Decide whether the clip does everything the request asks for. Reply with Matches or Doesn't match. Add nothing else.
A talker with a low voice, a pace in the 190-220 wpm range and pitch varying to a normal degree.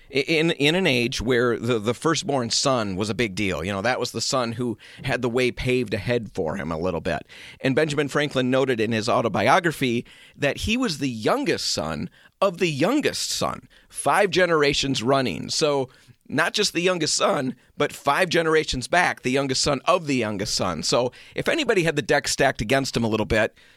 Matches